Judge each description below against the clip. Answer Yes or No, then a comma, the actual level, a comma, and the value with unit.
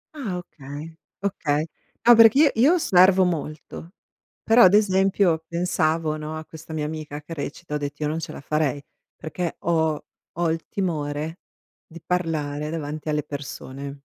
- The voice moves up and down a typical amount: Yes, average, 3.2 semitones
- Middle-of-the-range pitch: Yes, medium, 160 Hz